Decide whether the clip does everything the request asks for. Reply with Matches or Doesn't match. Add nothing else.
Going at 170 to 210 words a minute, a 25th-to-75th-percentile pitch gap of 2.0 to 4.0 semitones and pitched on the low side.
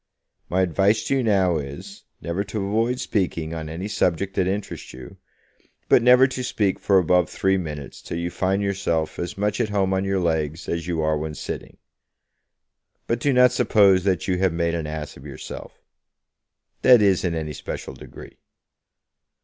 Matches